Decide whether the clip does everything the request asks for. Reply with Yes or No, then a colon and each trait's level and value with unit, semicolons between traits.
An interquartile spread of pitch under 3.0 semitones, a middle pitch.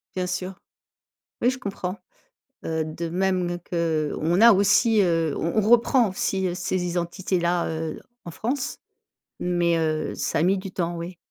Yes: narrow, 2.4 semitones; medium, 180 Hz